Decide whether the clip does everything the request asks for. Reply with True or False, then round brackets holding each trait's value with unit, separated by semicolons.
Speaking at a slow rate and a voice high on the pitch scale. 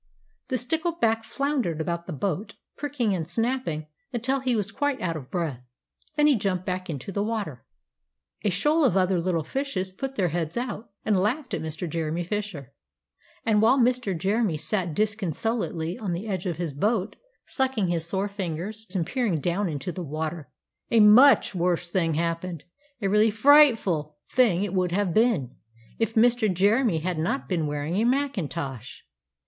False (170 wpm; 195 Hz)